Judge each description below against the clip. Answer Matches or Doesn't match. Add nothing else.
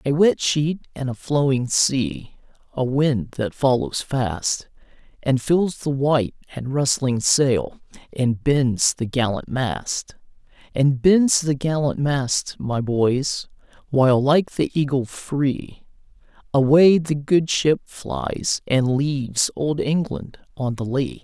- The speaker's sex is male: Matches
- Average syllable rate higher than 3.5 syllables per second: Doesn't match